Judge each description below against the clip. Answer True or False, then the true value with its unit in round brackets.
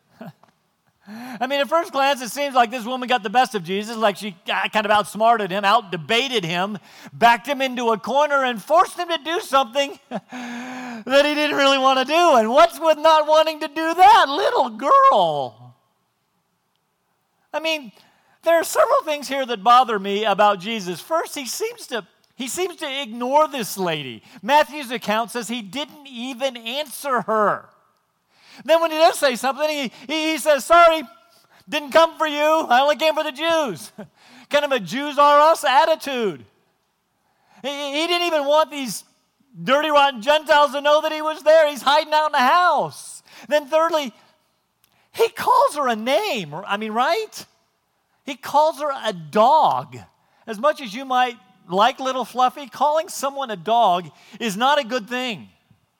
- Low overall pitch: False (275 Hz)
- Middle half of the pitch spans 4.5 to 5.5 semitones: True (5.1 semitones)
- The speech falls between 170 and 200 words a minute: True (175 wpm)